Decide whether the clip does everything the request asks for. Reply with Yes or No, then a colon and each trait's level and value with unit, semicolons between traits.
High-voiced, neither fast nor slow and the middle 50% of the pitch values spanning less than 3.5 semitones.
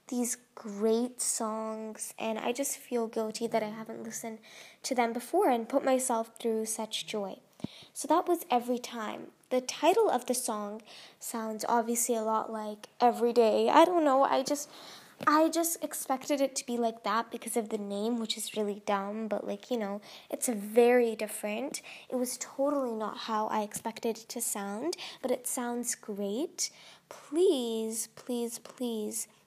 Yes: high, 235 Hz; average, 170 wpm; average, 2.9 semitones